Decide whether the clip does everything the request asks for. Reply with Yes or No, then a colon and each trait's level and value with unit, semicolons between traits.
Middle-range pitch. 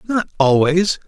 Yes: medium, 170 Hz